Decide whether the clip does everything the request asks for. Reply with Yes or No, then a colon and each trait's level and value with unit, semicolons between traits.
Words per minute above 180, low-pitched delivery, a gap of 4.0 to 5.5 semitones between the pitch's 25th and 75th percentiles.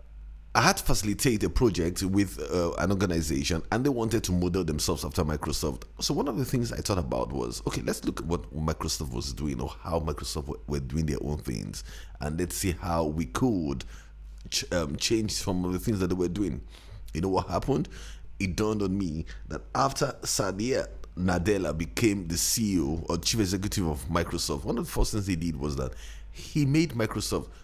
Yes: average, 200 wpm; very low, 85 Hz; average, 5.0 semitones